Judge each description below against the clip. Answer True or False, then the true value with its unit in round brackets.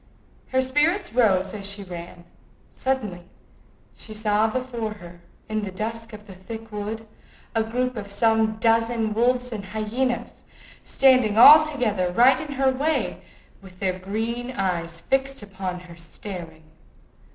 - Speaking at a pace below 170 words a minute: True (140 wpm)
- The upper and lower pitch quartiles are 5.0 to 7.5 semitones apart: False (4.4 semitones)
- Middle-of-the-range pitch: False (220 Hz)